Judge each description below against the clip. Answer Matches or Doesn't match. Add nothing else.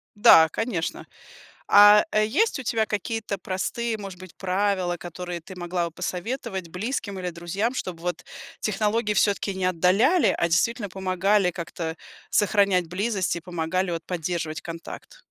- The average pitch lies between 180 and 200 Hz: Matches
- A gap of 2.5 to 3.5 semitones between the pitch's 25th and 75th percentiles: Matches